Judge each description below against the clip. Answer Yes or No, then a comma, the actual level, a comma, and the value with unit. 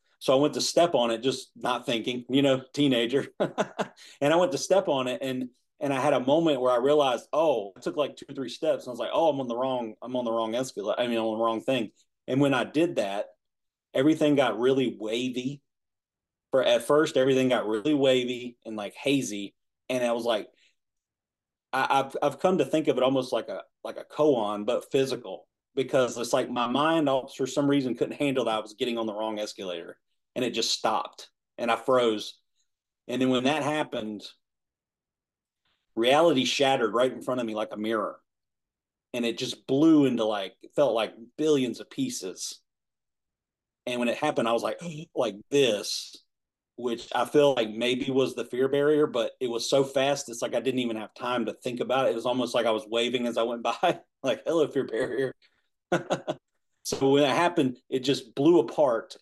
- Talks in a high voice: No, low, 130 Hz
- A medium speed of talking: No, fast, 210 wpm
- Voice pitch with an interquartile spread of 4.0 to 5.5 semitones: No, average, 3.5 semitones